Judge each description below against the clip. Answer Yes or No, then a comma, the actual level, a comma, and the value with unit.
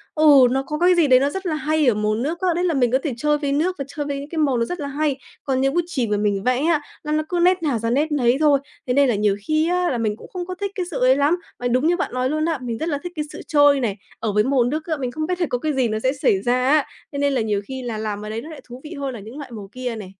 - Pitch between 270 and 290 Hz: Yes, very high, 275 Hz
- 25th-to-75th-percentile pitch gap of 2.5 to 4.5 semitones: Yes, average, 4.2 semitones